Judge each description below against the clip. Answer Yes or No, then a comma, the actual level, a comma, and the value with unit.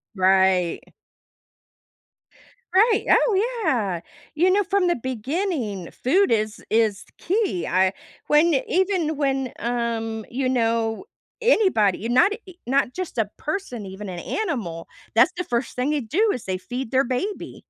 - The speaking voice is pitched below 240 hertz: No, very high, 250 Hz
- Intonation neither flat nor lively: No, wide, 8.9 semitones